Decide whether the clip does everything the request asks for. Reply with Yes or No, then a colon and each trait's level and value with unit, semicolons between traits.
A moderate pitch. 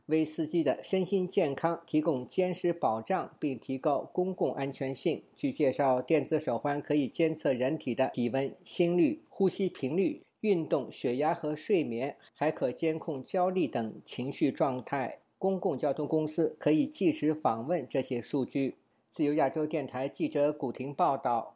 Yes: medium, 155 Hz